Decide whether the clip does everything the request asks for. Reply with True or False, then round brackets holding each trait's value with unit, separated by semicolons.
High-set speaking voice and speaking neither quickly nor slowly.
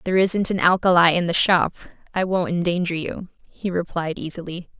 False (175 Hz; 175 wpm)